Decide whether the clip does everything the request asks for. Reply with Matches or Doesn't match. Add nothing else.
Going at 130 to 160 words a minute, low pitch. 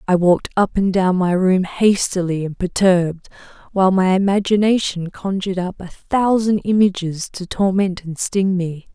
Doesn't match